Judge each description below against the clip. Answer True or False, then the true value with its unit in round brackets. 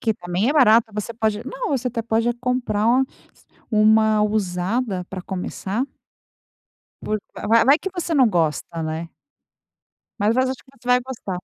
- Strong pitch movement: False (4.1 semitones)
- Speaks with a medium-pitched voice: False (220 Hz)